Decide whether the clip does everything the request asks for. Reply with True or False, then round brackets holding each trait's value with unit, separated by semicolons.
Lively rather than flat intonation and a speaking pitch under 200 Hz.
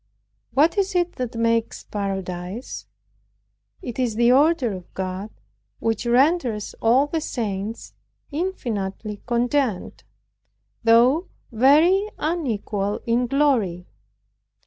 False (5.8 semitones; 235 Hz)